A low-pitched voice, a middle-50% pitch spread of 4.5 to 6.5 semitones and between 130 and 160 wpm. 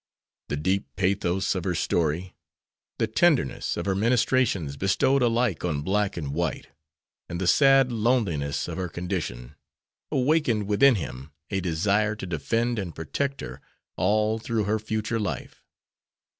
Yes: low, 100 Hz; average, 4.9 semitones; average, 145 wpm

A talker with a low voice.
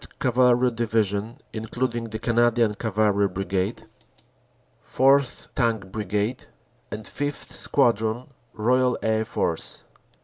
Yes: low, 115 Hz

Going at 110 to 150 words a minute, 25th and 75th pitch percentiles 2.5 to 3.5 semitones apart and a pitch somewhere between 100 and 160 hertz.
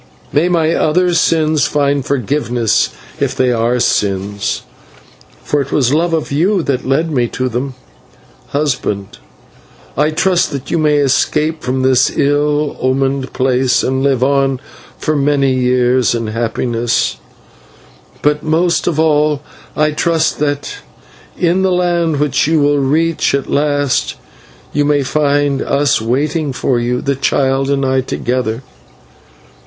Yes: average, 140 wpm; average, 2.9 semitones; medium, 140 Hz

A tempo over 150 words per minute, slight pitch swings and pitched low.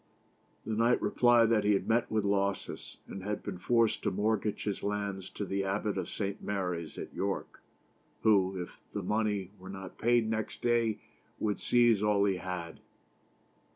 Yes: average, 170 wpm; narrow, 2.3 semitones; low, 100 Hz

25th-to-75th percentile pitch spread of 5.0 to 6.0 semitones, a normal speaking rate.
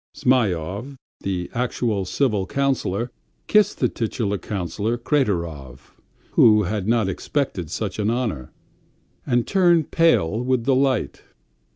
No: wide, 5.4 semitones; slow, 110 wpm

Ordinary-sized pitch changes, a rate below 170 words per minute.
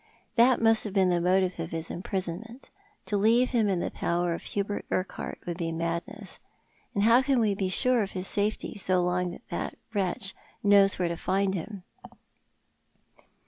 No: average, 3.2 semitones; average, 185 wpm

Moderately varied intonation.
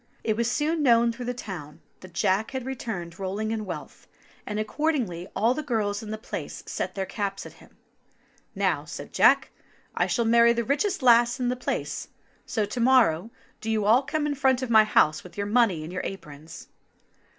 Yes: average, 4.1 semitones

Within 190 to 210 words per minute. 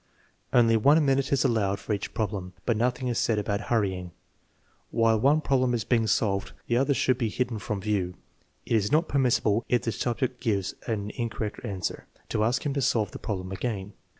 Yes: average, 195 wpm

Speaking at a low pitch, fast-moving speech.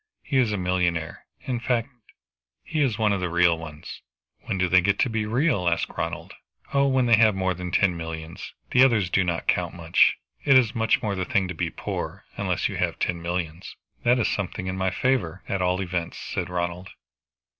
Yes: very low, 95 Hz; fast, 210 wpm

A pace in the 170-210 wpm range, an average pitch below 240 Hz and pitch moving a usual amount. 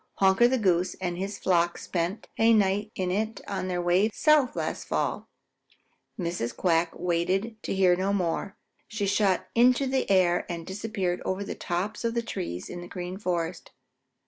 Yes: average, 175 wpm; high, 190 Hz; average, 3.3 semitones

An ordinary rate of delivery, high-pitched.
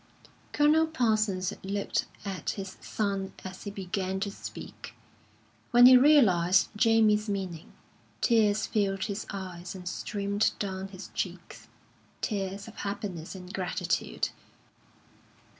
No: slow, 115 wpm; high, 200 Hz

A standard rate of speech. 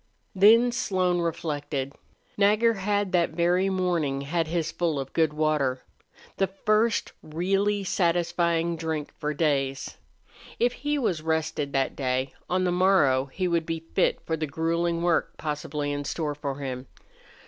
Yes: average, 150 wpm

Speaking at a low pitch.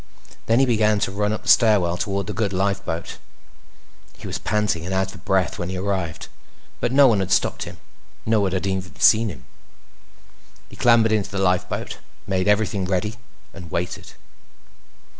Yes: low, 100 Hz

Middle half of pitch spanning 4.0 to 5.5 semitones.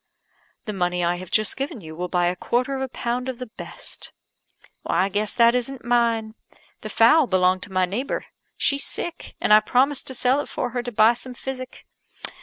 Yes: average, 5.1 semitones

